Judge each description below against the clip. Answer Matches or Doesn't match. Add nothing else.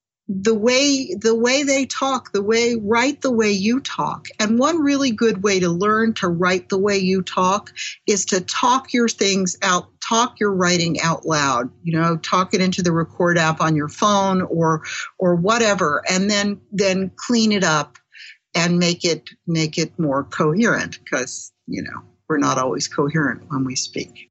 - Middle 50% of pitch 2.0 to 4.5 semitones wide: Doesn't match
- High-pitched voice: Matches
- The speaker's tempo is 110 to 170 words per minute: Doesn't match